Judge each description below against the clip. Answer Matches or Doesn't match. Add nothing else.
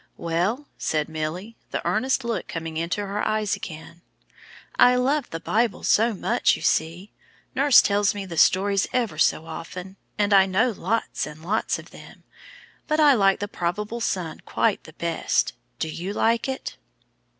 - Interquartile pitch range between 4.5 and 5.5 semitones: Matches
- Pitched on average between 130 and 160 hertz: Doesn't match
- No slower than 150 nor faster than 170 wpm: Matches